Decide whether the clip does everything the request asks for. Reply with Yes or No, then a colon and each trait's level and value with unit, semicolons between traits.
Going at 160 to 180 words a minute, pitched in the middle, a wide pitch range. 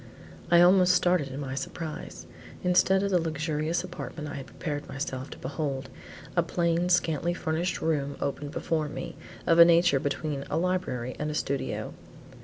No: average, 165 wpm; medium, 160 Hz; average, 3.6 semitones